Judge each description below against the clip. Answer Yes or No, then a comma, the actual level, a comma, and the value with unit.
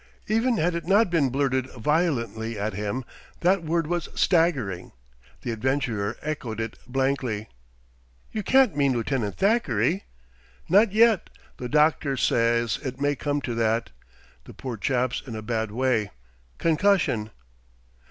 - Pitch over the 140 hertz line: No, low, 130 Hz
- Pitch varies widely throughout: Yes, wide, 6.5 semitones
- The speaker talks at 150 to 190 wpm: No, average, 140 wpm